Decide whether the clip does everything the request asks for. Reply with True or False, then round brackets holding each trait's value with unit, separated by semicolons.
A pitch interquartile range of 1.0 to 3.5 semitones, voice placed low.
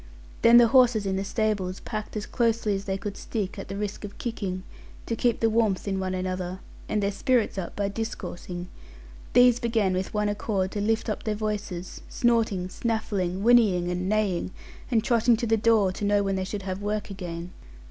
False (3.0 semitones; 205 Hz)